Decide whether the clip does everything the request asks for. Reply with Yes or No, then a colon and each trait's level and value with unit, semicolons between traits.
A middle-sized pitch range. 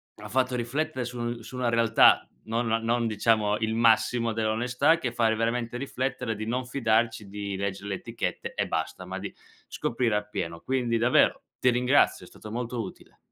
No: narrow, 2.2 semitones